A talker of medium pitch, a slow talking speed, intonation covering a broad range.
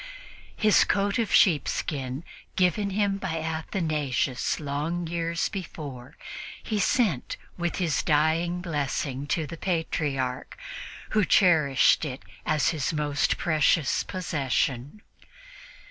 No: medium, 160 Hz; slow, 105 wpm; average, 4.0 semitones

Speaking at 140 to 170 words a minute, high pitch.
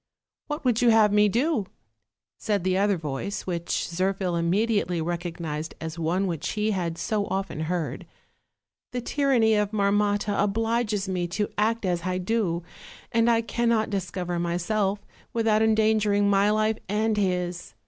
Yes: average, 150 wpm; high, 200 Hz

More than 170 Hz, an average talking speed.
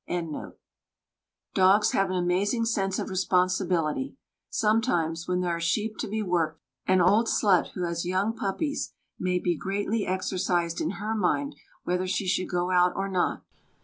Yes: medium, 185 Hz; average, 155 wpm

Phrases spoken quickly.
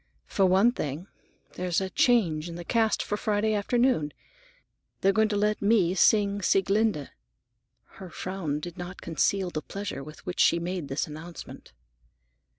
No: average, 155 wpm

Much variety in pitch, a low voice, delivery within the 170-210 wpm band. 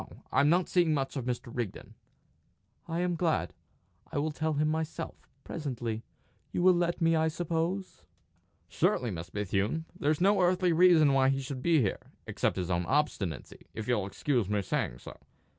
No: wide, 6.2 semitones; medium, 150 Hz; average, 175 wpm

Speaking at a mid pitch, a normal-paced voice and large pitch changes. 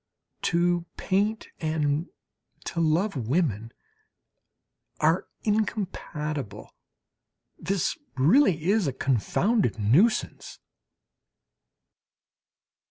No: medium, 165 Hz; slow, 65 wpm; wide, 5.7 semitones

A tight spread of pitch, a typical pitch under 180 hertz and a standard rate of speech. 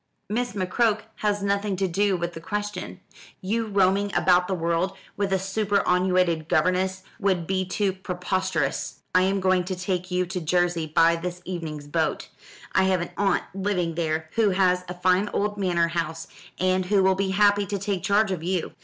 No: narrow, 2.1 semitones; medium, 185 Hz; average, 180 wpm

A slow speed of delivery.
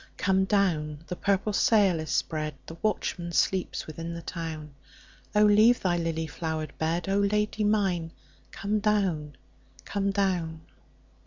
Yes: slow, 125 wpm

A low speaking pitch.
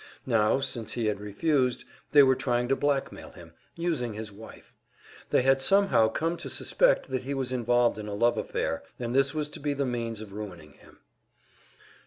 Yes: low, 125 Hz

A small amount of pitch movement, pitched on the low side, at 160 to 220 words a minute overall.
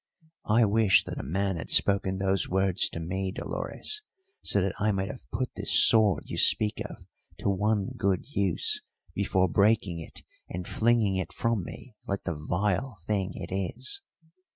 Yes: narrow, 2.2 semitones; low, 100 Hz; average, 170 wpm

